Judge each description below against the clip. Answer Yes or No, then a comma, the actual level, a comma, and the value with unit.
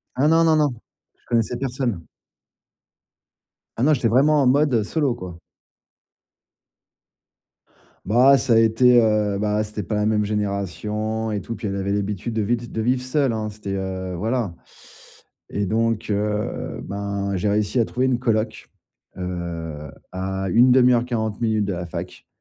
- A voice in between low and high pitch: No, low, 110 Hz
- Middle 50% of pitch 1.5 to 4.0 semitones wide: Yes, average, 3.6 semitones